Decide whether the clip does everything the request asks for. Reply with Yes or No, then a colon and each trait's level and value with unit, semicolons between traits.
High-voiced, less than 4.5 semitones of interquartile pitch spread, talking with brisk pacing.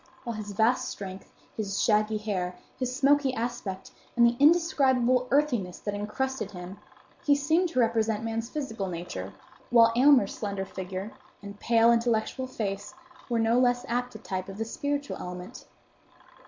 No: high, 230 Hz; average, 4.1 semitones; average, 155 wpm